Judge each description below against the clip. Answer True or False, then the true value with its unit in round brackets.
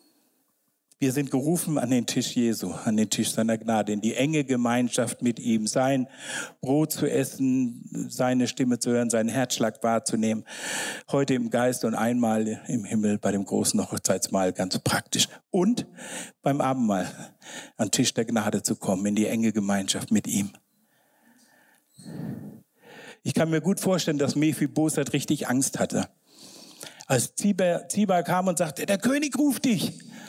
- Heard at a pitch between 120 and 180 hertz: True (135 Hz)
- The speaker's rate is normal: True (155 wpm)